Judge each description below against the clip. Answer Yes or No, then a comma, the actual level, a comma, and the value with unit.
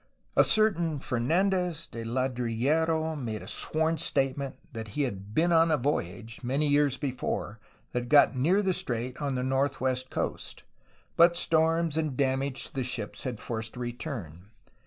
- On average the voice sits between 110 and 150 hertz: Yes, low, 135 Hz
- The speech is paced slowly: No, average, 155 wpm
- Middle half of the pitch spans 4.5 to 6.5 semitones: Yes, average, 4.8 semitones